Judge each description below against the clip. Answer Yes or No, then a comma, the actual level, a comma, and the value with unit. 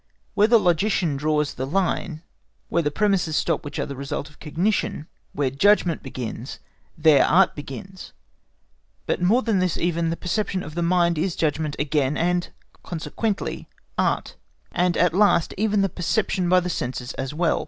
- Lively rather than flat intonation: No, average, 4.0 semitones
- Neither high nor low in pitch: Yes, medium, 170 Hz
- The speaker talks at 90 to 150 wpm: No, average, 165 wpm